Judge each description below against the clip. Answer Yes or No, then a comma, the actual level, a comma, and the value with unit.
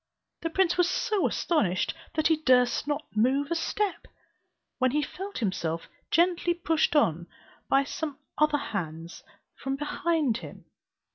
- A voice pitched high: Yes, very high, 295 Hz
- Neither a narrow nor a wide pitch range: No, wide, 5.7 semitones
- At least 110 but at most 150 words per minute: Yes, average, 140 wpm